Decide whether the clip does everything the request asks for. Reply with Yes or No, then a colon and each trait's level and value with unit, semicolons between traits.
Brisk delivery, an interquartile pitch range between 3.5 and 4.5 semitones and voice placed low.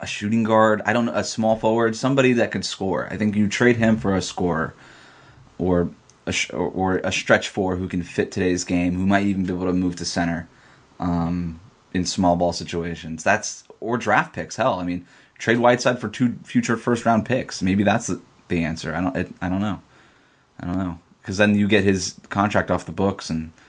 Yes: fast, 215 wpm; average, 3.8 semitones; very low, 95 Hz